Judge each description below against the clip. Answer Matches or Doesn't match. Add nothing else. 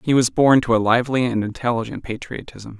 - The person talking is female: Doesn't match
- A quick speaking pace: Doesn't match